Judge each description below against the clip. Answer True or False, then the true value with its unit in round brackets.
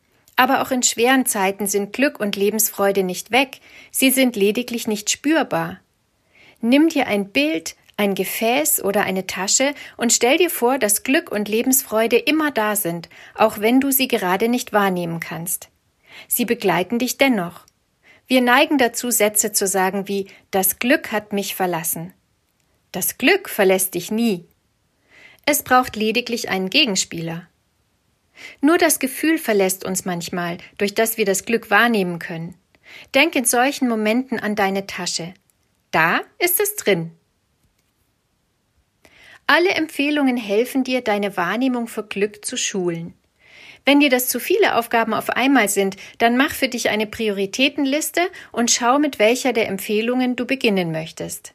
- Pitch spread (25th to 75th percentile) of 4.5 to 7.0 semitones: True (4.8 semitones)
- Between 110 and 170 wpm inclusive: True (150 wpm)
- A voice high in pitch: True (225 Hz)